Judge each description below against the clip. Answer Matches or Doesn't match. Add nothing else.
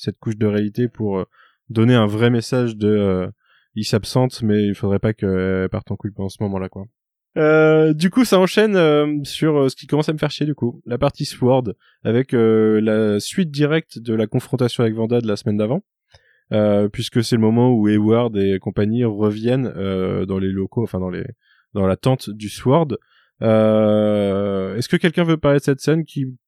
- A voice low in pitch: Matches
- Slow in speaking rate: Doesn't match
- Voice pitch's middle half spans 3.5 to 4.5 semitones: Matches